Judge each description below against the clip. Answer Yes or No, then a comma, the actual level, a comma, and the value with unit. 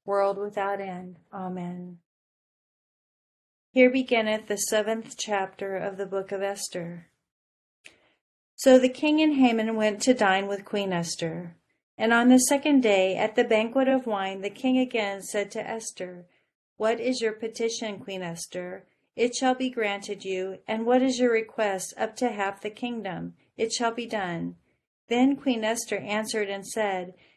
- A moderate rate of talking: Yes, average, 160 wpm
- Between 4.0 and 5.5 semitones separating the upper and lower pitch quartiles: No, average, 3.5 semitones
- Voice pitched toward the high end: Yes, high, 210 Hz